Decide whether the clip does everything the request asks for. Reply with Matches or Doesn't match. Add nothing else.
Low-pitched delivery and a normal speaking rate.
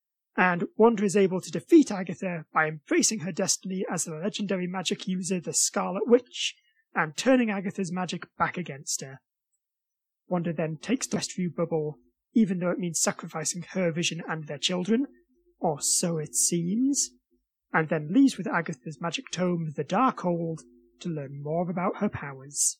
Doesn't match